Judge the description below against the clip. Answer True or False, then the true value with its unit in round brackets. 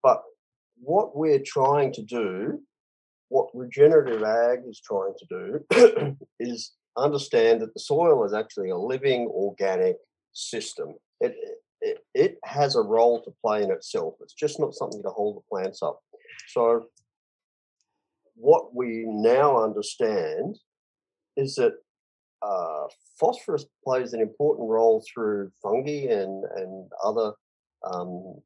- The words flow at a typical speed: False (130 wpm)